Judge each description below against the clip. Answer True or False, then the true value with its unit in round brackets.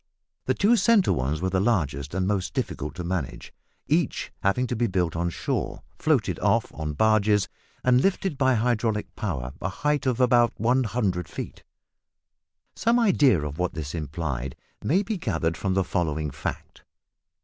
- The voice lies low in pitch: True (95 Hz)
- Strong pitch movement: True (7.3 semitones)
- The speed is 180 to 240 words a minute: False (160 wpm)